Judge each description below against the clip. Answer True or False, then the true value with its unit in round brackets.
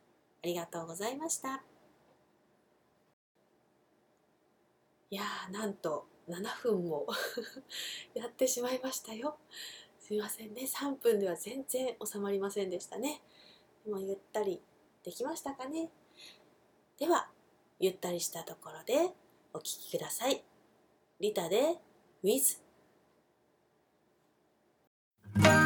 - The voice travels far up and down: True (6.2 semitones)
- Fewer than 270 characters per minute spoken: True (205 characters per minute)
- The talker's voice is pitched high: True (220 Hz)